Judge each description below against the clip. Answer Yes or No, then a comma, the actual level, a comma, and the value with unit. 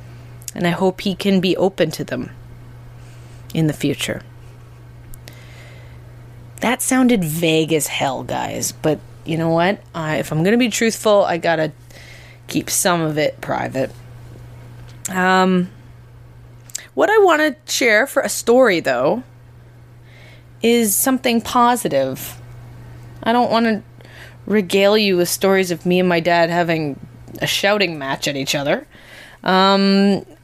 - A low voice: No, medium, 150 Hz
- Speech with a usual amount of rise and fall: No, wide, 7.8 semitones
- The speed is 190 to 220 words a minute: No, slow, 135 wpm